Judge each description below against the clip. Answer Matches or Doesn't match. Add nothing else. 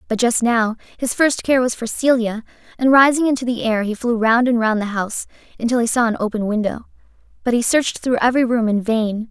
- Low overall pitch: Doesn't match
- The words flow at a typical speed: Doesn't match